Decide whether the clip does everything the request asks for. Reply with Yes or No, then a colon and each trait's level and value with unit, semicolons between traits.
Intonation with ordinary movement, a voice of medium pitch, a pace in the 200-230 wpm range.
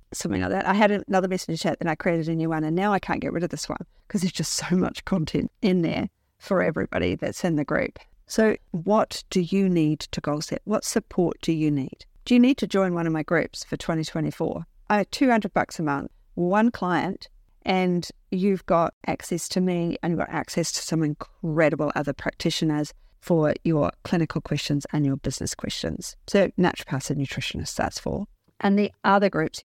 Yes: average, 3.6 semitones; medium, 175 Hz; fast, 205 wpm